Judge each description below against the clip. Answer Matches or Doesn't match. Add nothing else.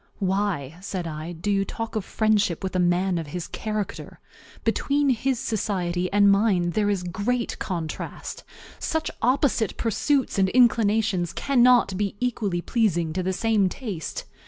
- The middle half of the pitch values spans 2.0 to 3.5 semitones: Doesn't match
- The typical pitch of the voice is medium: Doesn't match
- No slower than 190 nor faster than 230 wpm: Doesn't match